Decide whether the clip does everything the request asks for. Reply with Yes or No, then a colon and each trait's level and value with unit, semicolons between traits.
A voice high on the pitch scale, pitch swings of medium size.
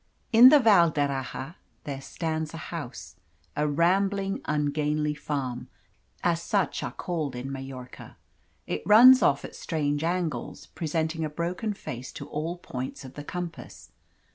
No: medium, 155 Hz; average, 3.9 semitones